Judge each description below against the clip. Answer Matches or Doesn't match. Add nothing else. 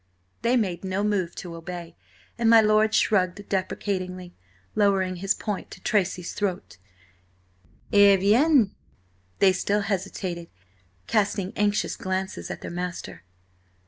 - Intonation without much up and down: Matches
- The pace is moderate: Doesn't match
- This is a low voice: Doesn't match